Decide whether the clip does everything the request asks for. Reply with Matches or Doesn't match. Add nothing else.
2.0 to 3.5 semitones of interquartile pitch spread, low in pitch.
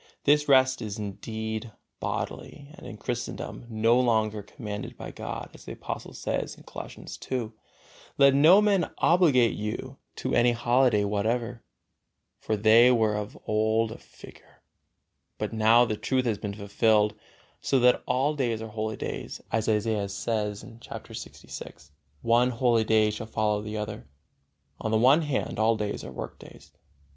Matches